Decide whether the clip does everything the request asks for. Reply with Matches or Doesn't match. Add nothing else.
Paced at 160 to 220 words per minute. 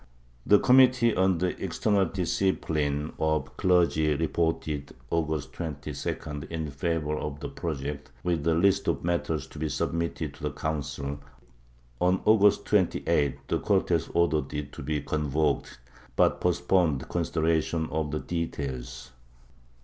Doesn't match